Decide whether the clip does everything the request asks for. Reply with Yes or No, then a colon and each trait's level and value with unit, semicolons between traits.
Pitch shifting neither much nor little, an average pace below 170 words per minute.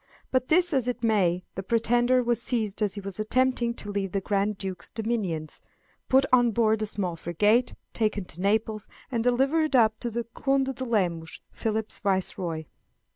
No: average, 3.7 semitones; average, 175 wpm